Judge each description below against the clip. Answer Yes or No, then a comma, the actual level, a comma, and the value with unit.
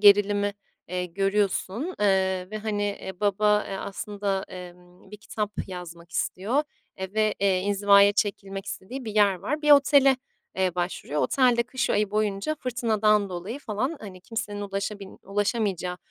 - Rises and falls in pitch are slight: Yes, narrow, 2.2 semitones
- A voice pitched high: Yes, high, 205 Hz